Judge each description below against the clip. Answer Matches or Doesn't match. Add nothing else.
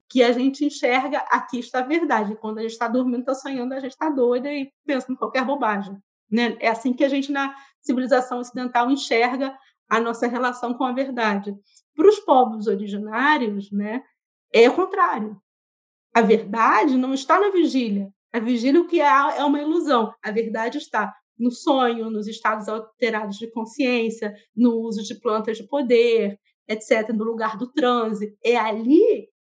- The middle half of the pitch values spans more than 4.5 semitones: Doesn't match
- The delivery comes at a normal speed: Matches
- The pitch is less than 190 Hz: Doesn't match